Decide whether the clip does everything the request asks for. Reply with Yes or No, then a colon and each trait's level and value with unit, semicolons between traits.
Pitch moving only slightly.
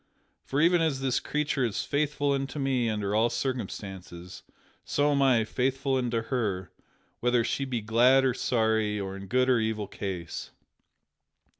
No: average, 4.2 semitones